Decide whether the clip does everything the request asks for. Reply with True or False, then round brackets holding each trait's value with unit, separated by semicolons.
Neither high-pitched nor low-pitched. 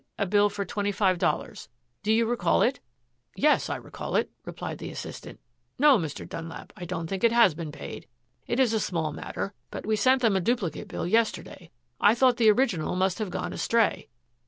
False (205 Hz)